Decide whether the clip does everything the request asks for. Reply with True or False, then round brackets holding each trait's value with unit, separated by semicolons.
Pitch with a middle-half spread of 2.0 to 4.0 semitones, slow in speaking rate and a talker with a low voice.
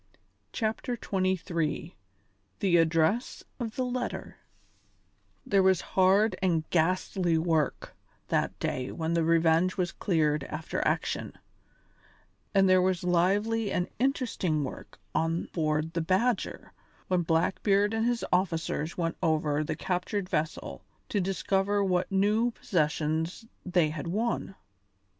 False (3.6 semitones; 120 wpm; 180 Hz)